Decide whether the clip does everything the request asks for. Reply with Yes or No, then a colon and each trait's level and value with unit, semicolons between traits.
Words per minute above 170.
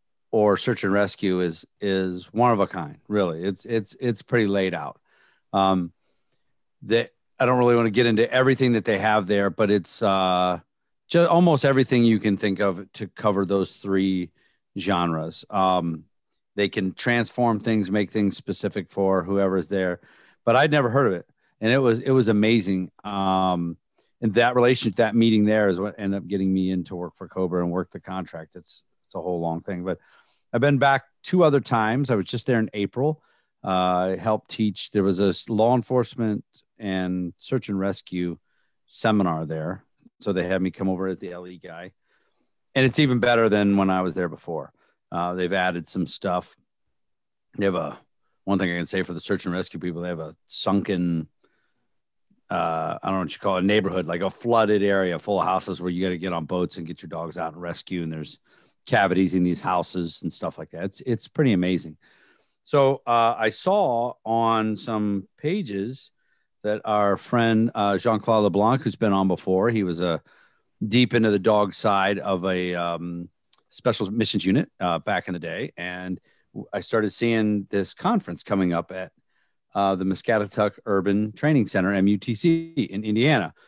Yes: average, 190 wpm